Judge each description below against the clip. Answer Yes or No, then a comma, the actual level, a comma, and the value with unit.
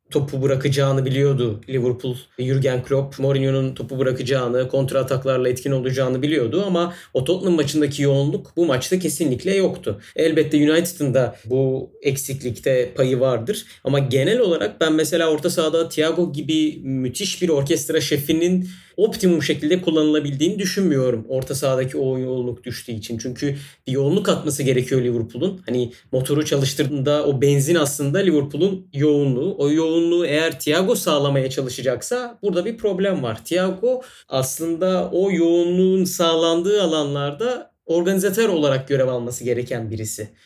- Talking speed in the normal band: Yes, average, 130 wpm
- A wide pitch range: No, average, 4.3 semitones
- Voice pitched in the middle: Yes, medium, 145 Hz